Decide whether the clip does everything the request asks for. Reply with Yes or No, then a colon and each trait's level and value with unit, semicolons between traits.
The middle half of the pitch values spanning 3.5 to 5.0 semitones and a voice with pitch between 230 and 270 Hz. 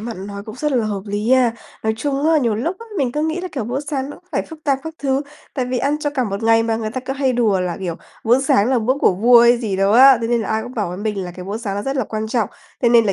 Yes: average, 4.0 semitones; high, 235 Hz